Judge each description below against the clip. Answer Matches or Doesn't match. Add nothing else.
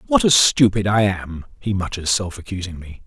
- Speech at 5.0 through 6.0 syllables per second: Matches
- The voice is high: Doesn't match